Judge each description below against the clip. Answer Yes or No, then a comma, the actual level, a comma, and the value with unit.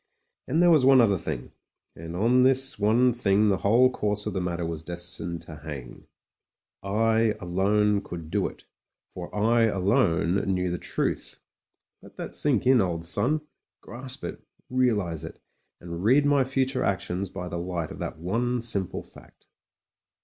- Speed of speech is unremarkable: Yes, average, 165 wpm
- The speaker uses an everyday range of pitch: No, wide, 6.0 semitones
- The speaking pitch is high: No, low, 100 Hz